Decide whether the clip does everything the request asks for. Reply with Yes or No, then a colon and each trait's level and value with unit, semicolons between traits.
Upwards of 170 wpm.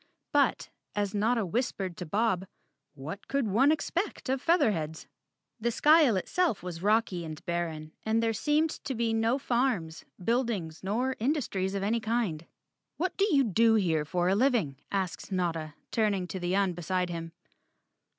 No: average, 160 wpm